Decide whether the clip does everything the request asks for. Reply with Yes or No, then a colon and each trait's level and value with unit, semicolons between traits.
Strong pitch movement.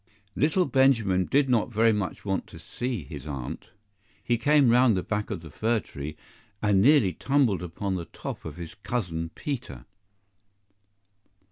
Yes: wide, 6.1 semitones